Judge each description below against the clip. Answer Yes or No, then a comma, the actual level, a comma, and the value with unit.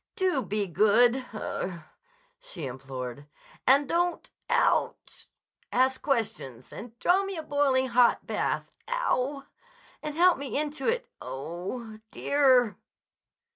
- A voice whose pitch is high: Yes, very high, 260 Hz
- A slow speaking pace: Yes, slow, 100 wpm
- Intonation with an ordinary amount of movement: No, wide, 6.6 semitones